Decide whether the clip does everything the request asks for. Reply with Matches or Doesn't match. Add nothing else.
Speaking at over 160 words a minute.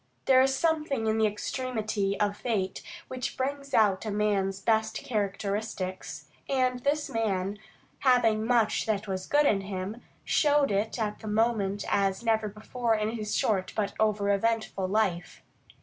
Doesn't match